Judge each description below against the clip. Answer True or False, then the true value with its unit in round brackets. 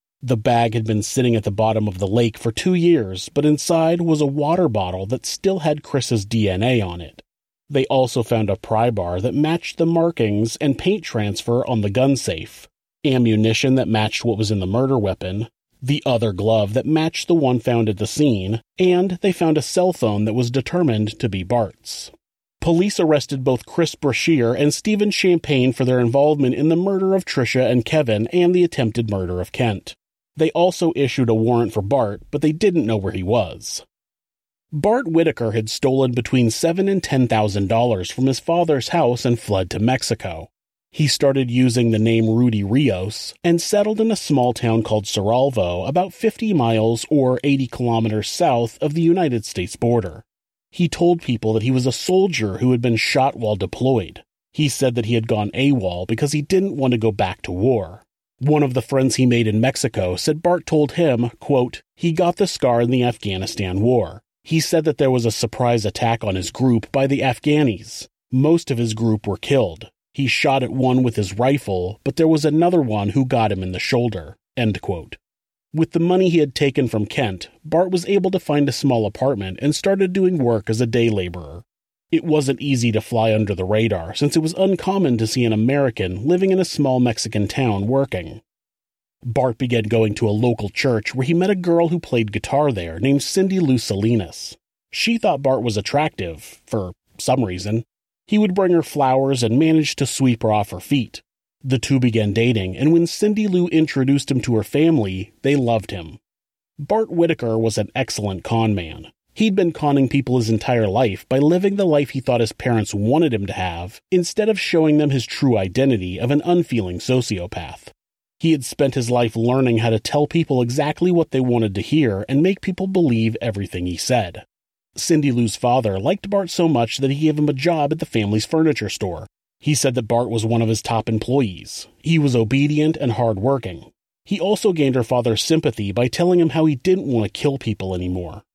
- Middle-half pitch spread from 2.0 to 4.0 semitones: False (5.6 semitones)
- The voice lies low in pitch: True (125 Hz)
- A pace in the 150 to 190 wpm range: False (200 wpm)